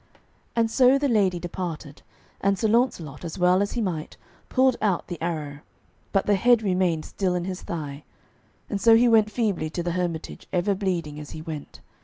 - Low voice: No, medium, 185 Hz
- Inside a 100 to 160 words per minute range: No, average, 190 wpm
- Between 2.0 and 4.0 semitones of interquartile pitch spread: No, average, 4.7 semitones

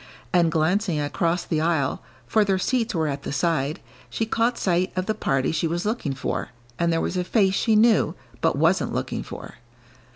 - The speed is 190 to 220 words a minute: Yes, average, 195 wpm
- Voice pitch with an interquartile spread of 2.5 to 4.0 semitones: No, average, 4.7 semitones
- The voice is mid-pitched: Yes, medium, 175 Hz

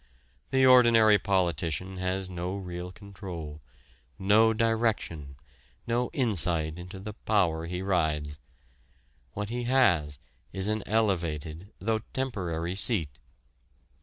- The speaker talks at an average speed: No, slow, 105 wpm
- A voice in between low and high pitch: No, very low, 95 Hz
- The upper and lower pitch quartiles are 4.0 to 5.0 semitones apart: Yes, average, 4.6 semitones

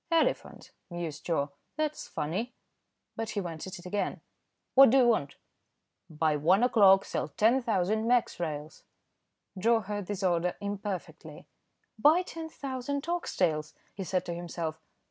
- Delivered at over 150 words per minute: No, average, 140 wpm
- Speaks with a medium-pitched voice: No, high, 195 Hz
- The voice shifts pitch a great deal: Yes, wide, 6.0 semitones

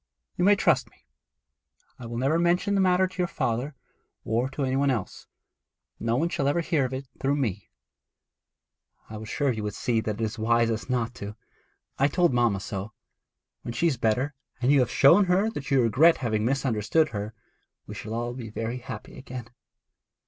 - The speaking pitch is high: No, low, 125 Hz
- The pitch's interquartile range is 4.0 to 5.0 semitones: Yes, average, 4.4 semitones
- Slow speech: No, average, 195 wpm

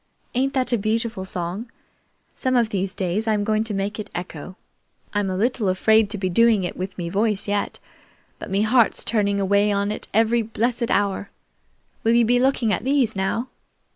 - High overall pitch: Yes, high, 210 Hz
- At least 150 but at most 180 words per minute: No, average, 190 wpm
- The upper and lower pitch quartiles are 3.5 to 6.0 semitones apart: No, average, 2.9 semitones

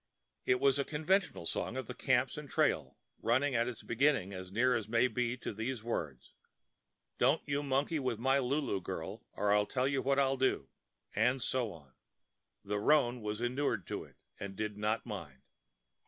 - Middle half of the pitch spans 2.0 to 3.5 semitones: No, average, 4.5 semitones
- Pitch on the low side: Yes, low, 120 Hz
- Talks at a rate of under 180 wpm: No, average, 185 wpm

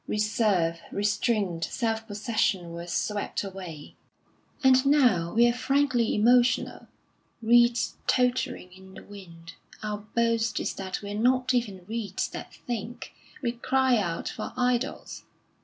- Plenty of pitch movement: No, average, 4.2 semitones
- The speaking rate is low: Yes, slow, 130 wpm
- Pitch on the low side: No, high, 220 Hz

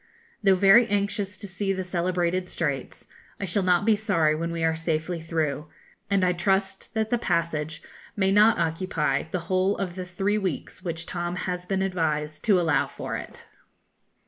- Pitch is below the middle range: No, medium, 180 Hz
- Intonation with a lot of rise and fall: No, average, 3.0 semitones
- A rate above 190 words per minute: No, average, 175 wpm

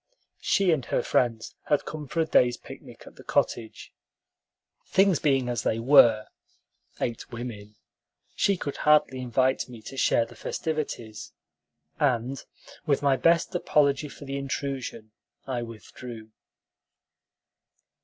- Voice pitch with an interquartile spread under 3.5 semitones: No, average, 3.9 semitones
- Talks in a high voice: No, low, 130 Hz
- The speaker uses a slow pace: Yes, slow, 130 wpm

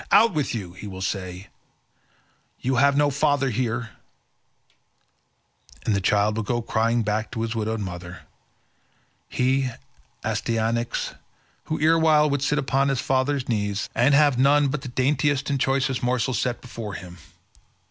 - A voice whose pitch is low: Yes, low, 125 Hz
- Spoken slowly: No, average, 145 wpm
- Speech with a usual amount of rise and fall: Yes, average, 4.3 semitones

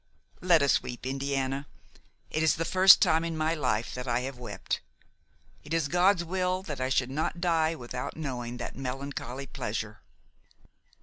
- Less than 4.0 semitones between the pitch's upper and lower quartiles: No, average, 4.3 semitones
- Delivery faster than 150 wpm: Yes, average, 165 wpm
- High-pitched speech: No, medium, 140 Hz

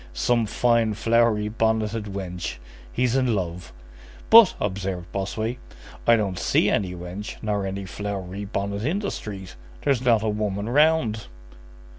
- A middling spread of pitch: Yes, average, 3.2 semitones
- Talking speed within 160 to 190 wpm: No, average, 140 wpm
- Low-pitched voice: Yes, low, 105 Hz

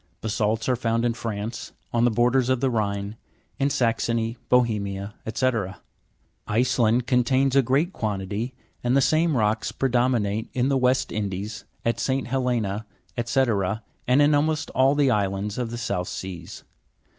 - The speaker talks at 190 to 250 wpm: No, average, 150 wpm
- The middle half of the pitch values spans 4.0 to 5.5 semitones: No, average, 3.5 semitones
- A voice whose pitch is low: Yes, low, 120 Hz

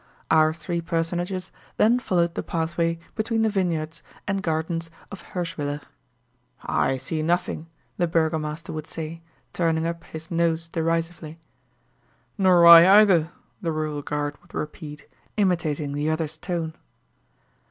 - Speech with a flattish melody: Yes, narrow, 1.9 semitones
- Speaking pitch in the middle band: Yes, medium, 165 Hz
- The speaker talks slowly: Yes, slow, 130 wpm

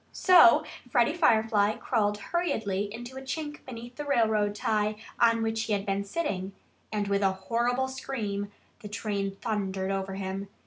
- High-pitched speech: Yes, high, 215 Hz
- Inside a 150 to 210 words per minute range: Yes, average, 160 wpm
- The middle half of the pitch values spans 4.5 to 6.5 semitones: No, average, 3.3 semitones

